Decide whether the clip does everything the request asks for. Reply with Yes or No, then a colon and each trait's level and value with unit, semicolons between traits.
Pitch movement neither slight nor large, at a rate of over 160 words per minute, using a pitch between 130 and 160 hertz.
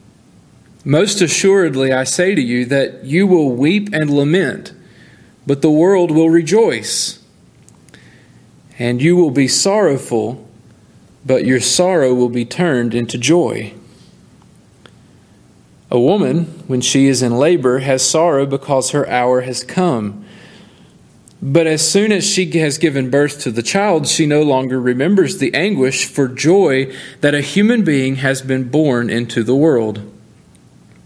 No: average, 4.8 semitones; average, 140 wpm; medium, 140 Hz